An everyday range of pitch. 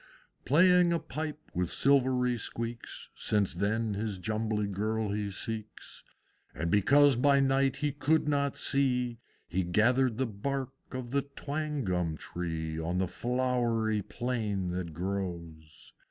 No: wide, 5.7 semitones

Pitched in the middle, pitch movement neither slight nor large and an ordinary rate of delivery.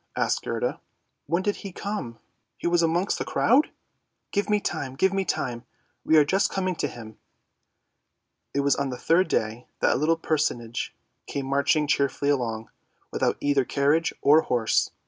No: medium, 145 Hz; wide, 5.7 semitones; average, 180 wpm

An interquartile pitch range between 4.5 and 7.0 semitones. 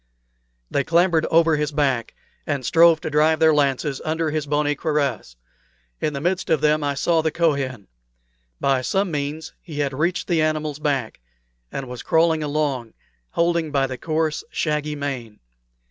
No: narrow, 2.4 semitones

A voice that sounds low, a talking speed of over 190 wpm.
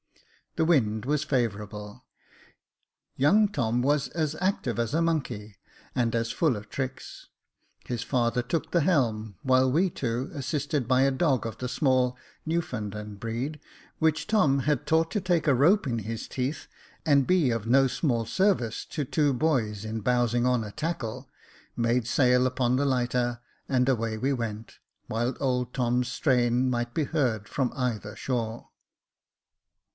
No: low, 125 Hz; average, 155 wpm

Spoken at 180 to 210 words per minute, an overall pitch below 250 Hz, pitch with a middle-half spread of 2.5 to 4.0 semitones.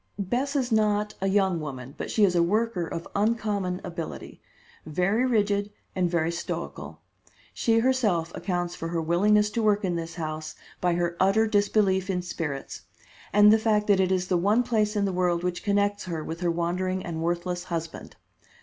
Yes: average, 185 wpm; medium, 185 Hz; average, 3.4 semitones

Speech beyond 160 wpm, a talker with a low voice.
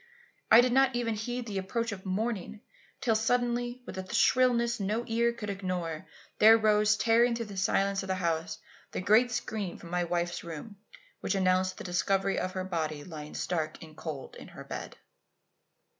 No: average, 180 wpm; high, 200 Hz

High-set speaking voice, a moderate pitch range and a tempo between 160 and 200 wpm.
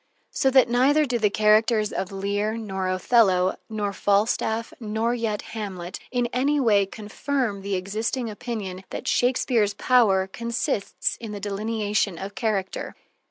No: high, 215 Hz; average, 3.0 semitones; average, 140 wpm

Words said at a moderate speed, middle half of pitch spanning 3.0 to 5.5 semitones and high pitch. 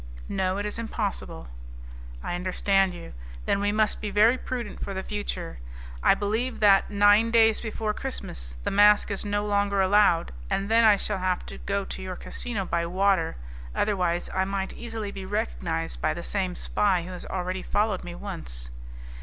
No: average, 180 wpm; narrow, 2.4 semitones; high, 200 Hz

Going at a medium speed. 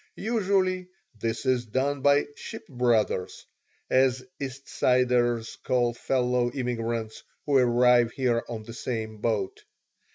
No: slow, 120 wpm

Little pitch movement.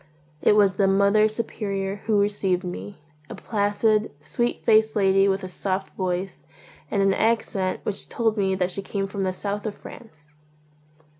Yes: narrow, 1.7 semitones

